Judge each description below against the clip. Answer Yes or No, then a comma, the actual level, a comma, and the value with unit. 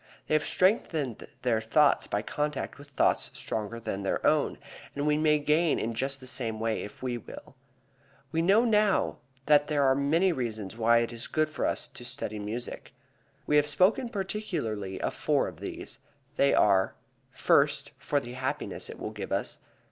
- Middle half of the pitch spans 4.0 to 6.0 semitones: Yes, average, 5.2 semitones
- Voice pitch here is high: No, medium, 140 Hz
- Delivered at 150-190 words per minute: Yes, average, 180 wpm